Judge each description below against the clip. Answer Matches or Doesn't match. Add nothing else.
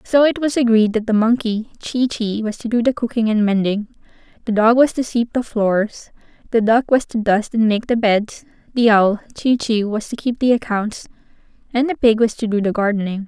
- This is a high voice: Matches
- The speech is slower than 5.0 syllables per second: Doesn't match